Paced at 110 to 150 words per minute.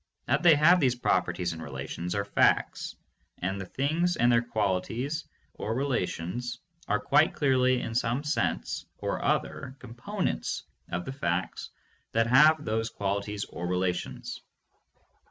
Yes: slow, 135 wpm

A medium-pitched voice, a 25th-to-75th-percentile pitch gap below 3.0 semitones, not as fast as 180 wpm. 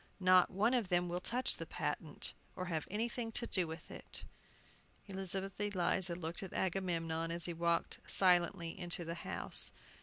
Yes: medium, 180 Hz; narrow, 2.4 semitones; average, 160 wpm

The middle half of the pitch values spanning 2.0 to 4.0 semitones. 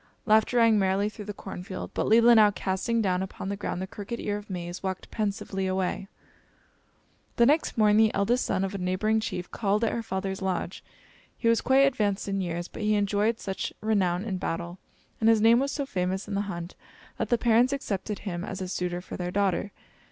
Yes: average, 2.8 semitones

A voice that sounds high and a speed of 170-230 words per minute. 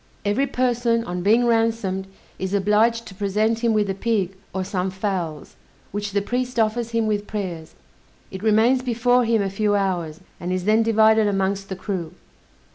Yes: high, 210 Hz; average, 175 wpm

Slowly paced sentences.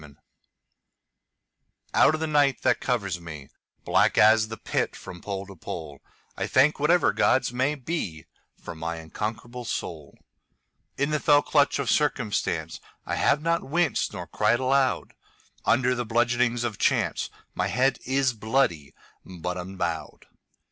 Yes: slow, 125 wpm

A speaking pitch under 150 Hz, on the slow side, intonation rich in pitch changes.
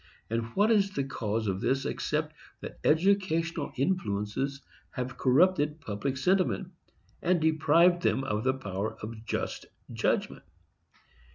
Yes: medium, 140 Hz; slow, 125 wpm; wide, 7.0 semitones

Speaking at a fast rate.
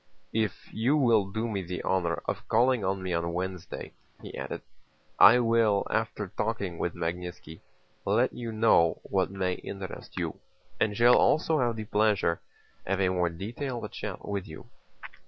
No: average, 160 wpm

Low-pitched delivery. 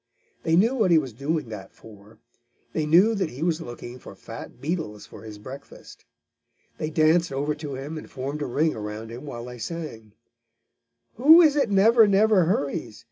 No: medium, 150 Hz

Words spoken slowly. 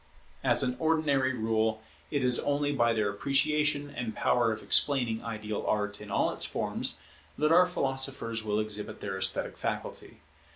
No: average, 160 wpm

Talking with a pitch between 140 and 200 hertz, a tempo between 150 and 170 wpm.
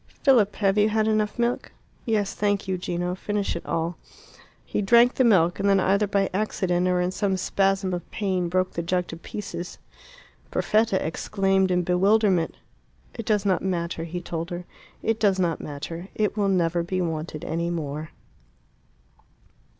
Yes: high, 190 Hz; average, 165 wpm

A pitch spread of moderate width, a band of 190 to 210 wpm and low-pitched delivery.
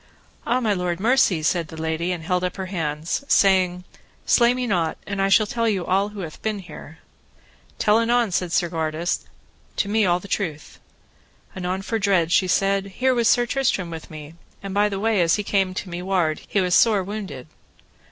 No: average, 3.3 semitones; average, 200 wpm; high, 190 Hz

